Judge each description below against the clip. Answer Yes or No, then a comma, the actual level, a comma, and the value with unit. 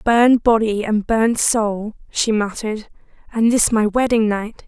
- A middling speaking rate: Yes, average, 155 wpm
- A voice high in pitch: Yes, high, 220 Hz